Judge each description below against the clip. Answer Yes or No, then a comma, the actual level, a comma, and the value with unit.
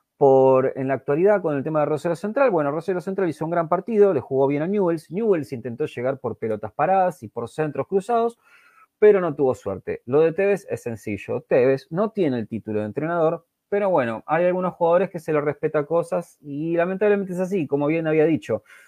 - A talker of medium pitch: Yes, medium, 165 Hz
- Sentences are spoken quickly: Yes, fast, 210 wpm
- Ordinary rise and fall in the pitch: No, wide, 5.9 semitones